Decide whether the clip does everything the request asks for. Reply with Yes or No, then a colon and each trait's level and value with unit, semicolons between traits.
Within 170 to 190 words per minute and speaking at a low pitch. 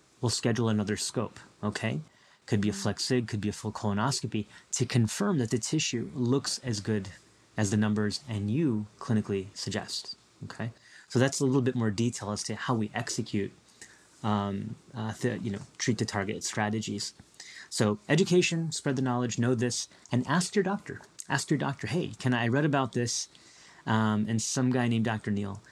Yes: average, 180 wpm; low, 115 Hz